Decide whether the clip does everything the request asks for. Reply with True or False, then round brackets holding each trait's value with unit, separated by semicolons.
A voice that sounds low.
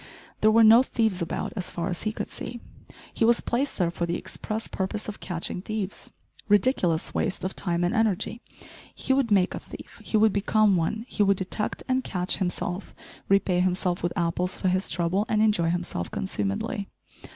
False (195 Hz)